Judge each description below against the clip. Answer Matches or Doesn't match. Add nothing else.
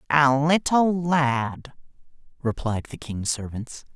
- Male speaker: Matches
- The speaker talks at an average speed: Doesn't match